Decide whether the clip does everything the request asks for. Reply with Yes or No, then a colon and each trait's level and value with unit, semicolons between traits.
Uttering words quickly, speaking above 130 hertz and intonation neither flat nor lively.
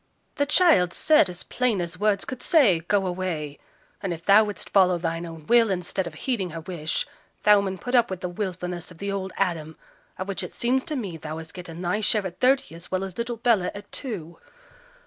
Yes: fast, 220 wpm; medium, 185 Hz; average, 3.9 semitones